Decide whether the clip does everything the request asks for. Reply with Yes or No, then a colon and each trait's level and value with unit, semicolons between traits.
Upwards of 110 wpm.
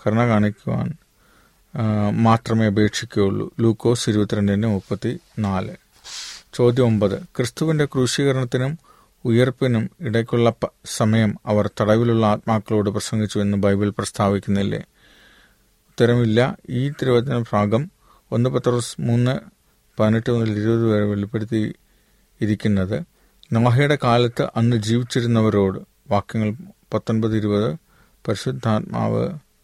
No: average, 85 wpm